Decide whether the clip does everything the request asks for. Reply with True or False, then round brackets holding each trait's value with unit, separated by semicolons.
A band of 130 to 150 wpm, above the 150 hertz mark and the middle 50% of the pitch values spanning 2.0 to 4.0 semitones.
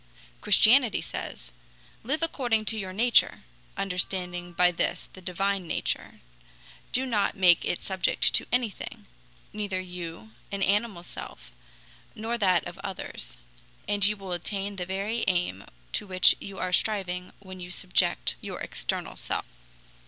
True (140 wpm; 190 Hz; 2.6 semitones)